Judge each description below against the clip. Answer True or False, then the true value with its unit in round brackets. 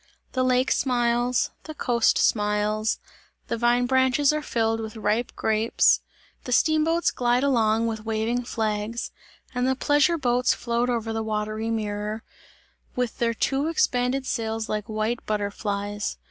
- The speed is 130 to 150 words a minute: True (140 wpm)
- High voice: True (235 Hz)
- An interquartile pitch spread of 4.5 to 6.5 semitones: False (2.6 semitones)